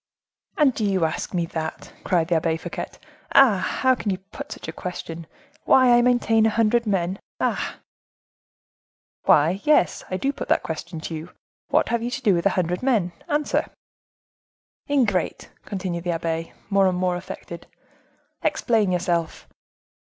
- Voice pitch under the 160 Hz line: No, medium, 185 Hz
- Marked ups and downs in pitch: Yes, wide, 5.7 semitones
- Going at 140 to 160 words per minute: Yes, average, 155 wpm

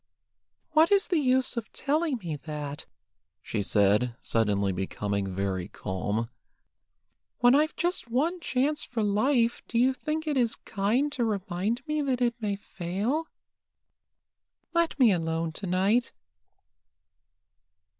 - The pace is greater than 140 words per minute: No, slow, 135 wpm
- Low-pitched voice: No, high, 225 Hz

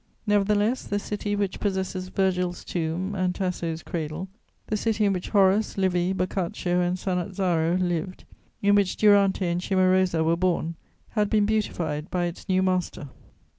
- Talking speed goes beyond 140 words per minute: Yes, average, 150 wpm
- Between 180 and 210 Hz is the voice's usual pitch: Yes, medium, 185 Hz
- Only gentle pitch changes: Yes, narrow, 2.3 semitones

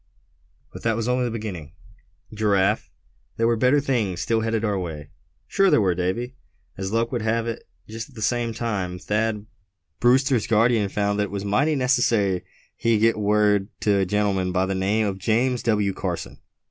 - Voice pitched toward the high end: No, low, 110 Hz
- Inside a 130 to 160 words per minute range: No, average, 185 wpm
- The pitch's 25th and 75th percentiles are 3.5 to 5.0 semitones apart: No, average, 2.9 semitones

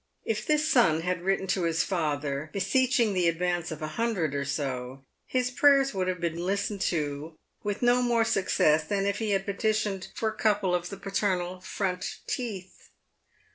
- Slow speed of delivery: No, average, 175 wpm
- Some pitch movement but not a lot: Yes, average, 4.6 semitones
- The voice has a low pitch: No, high, 190 Hz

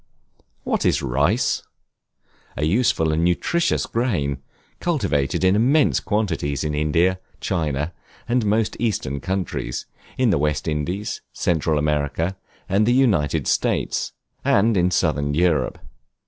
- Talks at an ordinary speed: No, slow, 120 wpm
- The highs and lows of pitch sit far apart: Yes, wide, 6.3 semitones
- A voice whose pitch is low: Yes, very low, 85 Hz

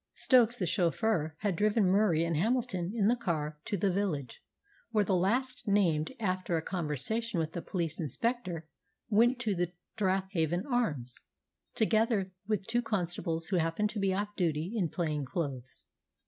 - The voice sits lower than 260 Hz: Yes, medium, 185 Hz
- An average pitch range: Yes, average, 4.7 semitones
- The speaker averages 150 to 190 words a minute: Yes, average, 160 wpm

